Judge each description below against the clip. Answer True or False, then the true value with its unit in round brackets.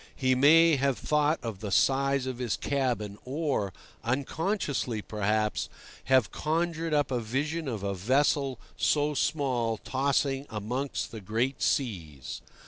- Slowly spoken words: True (125 wpm)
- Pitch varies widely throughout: False (4.7 semitones)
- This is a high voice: False (130 Hz)